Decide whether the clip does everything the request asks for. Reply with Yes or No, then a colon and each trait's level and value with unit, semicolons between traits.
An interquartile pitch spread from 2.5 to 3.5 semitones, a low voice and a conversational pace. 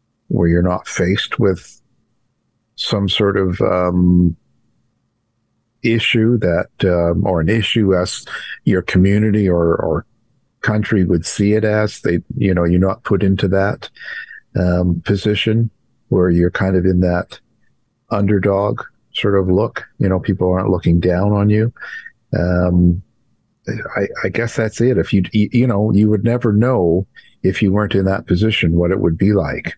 Yes: average, 3.0 semitones; very low, 95 Hz; average, 155 wpm